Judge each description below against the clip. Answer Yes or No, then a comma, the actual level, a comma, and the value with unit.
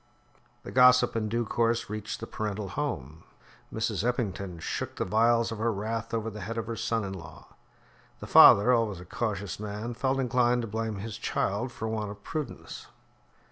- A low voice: Yes, low, 110 Hz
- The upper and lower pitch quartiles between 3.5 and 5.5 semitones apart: No, narrow, 2.5 semitones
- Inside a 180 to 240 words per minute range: Yes, average, 185 wpm